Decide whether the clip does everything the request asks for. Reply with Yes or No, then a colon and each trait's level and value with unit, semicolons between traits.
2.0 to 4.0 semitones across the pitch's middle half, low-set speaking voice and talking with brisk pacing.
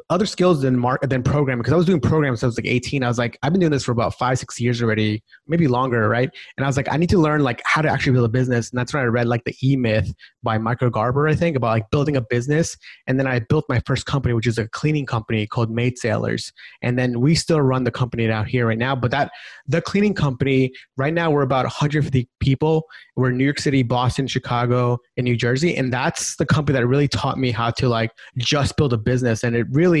Yes: average, 3.3 semitones; low, 130 Hz; fast, 265 wpm